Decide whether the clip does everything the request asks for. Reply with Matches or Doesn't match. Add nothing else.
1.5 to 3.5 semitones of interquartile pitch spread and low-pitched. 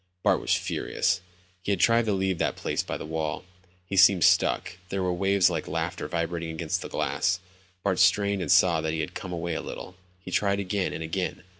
Matches